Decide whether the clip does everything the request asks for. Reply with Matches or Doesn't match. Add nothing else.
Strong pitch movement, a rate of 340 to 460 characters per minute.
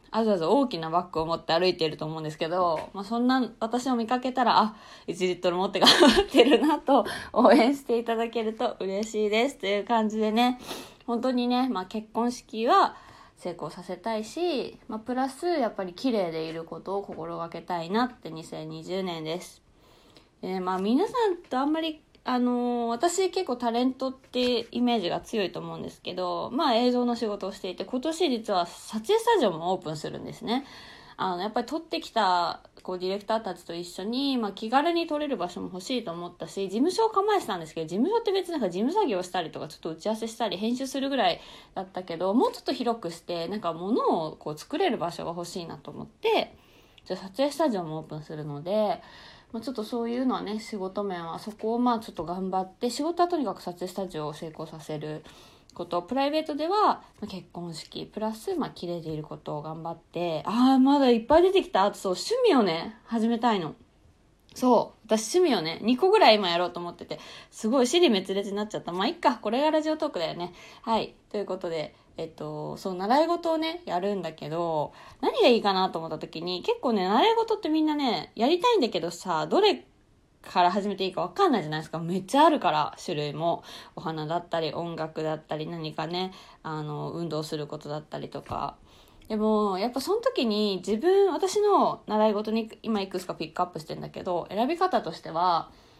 Matches